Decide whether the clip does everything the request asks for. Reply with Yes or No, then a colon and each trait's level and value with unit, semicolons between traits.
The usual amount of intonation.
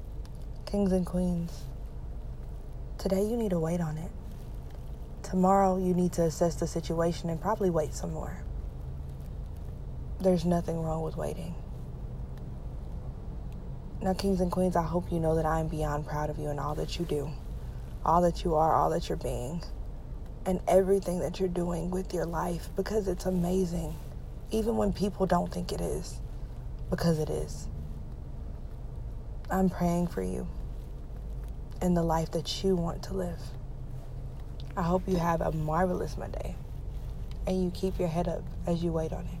Yes: average, 4.0 semitones